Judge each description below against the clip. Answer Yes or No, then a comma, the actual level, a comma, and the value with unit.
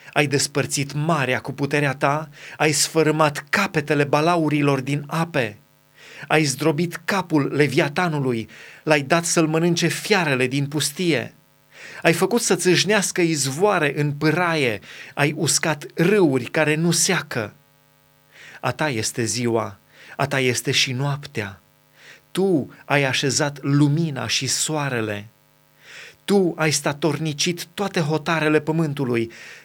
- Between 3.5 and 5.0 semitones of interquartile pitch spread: No, average, 3.1 semitones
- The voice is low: No, medium, 150 Hz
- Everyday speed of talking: No, slow, 110 wpm